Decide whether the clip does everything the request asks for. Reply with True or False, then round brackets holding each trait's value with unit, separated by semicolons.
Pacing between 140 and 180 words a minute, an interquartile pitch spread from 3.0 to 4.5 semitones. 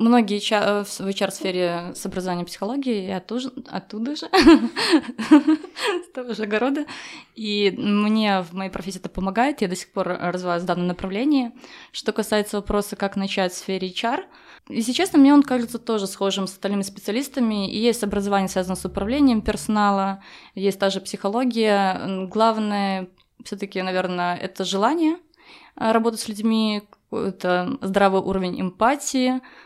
True (150 wpm; 3.9 semitones)